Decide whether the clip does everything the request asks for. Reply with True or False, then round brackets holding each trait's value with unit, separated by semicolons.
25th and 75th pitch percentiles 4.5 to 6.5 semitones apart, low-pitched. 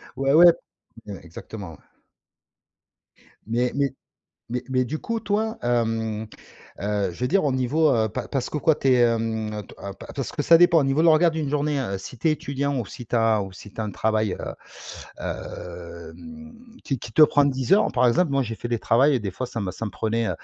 True (5.1 semitones; 125 Hz)